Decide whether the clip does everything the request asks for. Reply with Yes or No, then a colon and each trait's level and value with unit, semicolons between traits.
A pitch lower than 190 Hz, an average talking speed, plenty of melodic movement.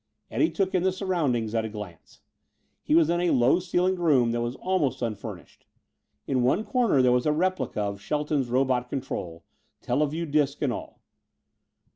Yes: medium, 140 Hz; average, 170 wpm; wide, 6.4 semitones